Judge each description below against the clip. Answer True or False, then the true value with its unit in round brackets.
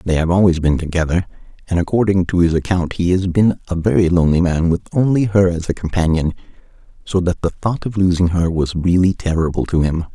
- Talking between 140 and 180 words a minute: False (205 wpm)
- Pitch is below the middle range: True (90 Hz)